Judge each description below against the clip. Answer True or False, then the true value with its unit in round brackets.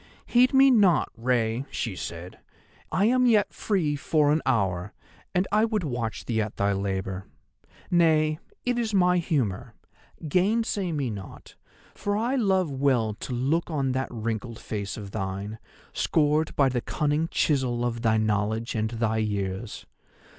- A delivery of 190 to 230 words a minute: False (155 wpm)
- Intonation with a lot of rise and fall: True (8.1 semitones)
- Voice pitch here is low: True (130 Hz)